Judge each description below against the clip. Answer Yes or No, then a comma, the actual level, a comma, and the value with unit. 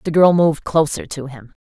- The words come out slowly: No, fast, 220 wpm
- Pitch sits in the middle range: Yes, medium, 155 Hz